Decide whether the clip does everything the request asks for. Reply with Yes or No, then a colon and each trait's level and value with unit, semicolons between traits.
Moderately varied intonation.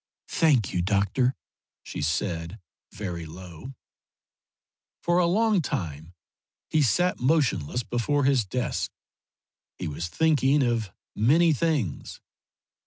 No: wide, 9.0 semitones